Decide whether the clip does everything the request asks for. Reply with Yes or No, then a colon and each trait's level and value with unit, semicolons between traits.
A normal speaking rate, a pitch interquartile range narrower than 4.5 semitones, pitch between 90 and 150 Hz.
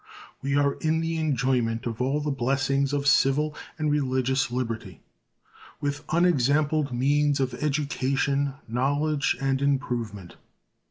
No: slow, 120 wpm; narrow, 2.4 semitones; medium, 140 Hz